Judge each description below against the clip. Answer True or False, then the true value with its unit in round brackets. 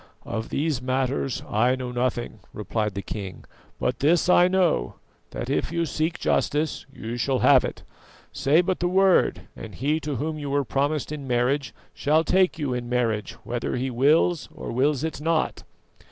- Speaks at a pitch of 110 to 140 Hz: True (135 Hz)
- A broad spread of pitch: False (4.5 semitones)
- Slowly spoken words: False (175 wpm)